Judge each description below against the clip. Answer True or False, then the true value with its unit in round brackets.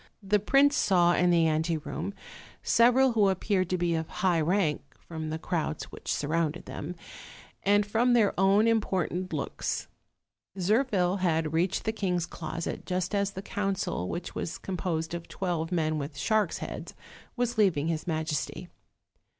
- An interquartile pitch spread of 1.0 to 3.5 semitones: False (3.9 semitones)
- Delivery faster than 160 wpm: False (150 wpm)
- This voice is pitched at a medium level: True (180 Hz)